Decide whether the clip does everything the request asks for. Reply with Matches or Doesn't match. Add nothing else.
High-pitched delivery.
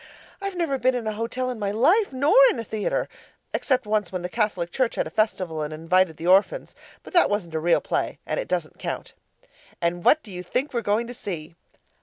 Matches